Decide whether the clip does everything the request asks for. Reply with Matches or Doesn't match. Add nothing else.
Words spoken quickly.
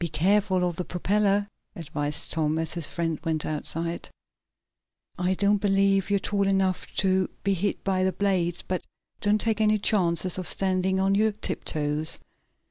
Doesn't match